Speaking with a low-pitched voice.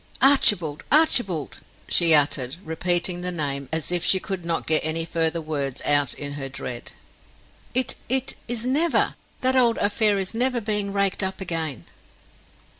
No: medium, 175 Hz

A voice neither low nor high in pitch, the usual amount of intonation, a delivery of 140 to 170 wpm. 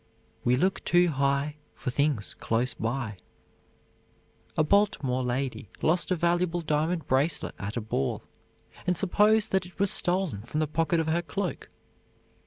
No: medium, 155 Hz; wide, 5.7 semitones; average, 150 wpm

